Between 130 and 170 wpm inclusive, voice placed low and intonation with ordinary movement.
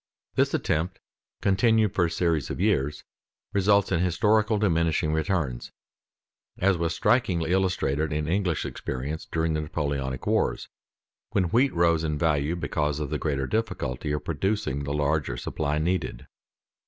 Yes: average, 140 wpm; very low, 80 Hz; average, 4.2 semitones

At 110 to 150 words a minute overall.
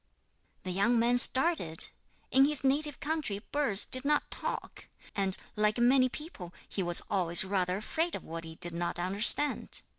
No: average, 160 wpm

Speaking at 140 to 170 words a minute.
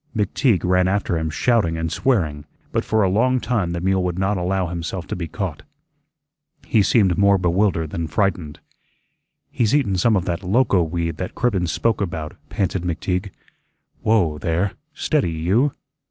Yes: average, 165 wpm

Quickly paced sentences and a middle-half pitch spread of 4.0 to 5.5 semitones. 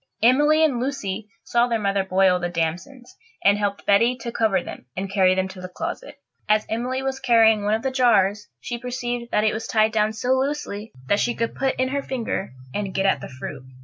Yes: fast, 215 wpm; average, 4.3 semitones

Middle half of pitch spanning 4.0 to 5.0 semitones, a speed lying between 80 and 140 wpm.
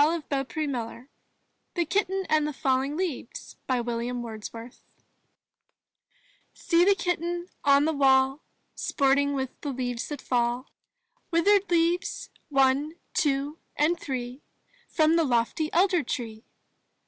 Yes: average, 4.7 semitones; slow, 135 wpm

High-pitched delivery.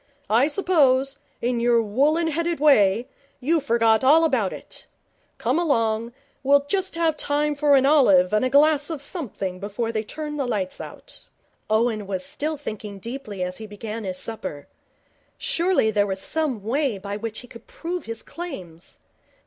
Yes: high, 245 Hz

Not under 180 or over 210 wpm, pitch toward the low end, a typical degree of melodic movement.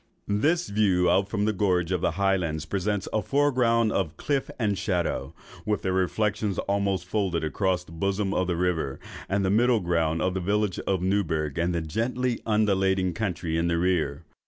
Yes: average, 185 wpm; very low, 95 Hz; average, 3.4 semitones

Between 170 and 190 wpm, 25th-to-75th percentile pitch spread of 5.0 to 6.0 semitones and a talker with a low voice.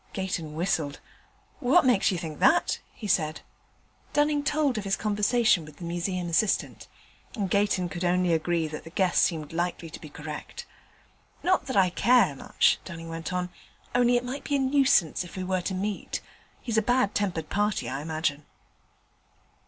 No: average, 175 wpm; average, 5.3 semitones; medium, 185 Hz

